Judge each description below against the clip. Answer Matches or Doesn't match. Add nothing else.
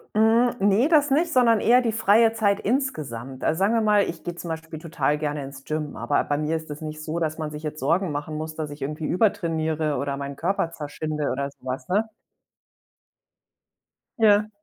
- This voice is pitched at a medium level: Matches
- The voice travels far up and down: Matches